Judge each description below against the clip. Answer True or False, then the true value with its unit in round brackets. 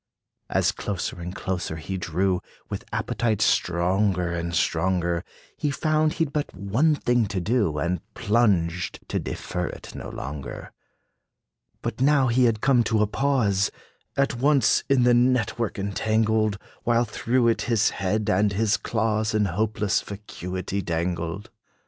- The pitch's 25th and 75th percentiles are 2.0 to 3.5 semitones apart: False (4.8 semitones)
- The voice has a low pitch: True (105 Hz)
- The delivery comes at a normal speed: True (150 wpm)